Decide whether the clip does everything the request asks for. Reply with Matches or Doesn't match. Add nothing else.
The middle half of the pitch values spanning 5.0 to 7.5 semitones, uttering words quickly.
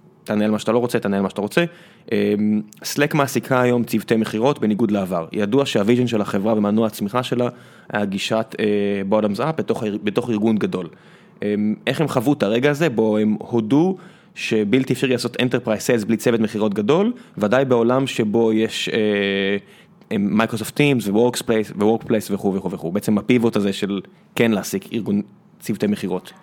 Doesn't match